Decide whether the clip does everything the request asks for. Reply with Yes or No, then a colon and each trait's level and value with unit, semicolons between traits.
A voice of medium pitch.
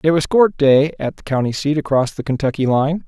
Yes: medium, 145 Hz